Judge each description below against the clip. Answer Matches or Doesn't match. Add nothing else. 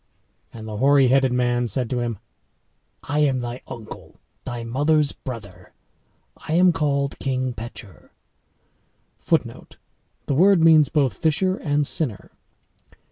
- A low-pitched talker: Matches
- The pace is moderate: Doesn't match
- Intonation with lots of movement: Doesn't match